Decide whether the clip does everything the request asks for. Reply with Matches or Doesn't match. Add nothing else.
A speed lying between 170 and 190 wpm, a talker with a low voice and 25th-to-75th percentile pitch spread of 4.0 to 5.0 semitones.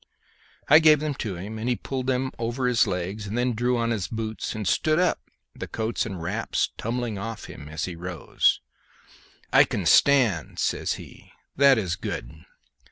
Matches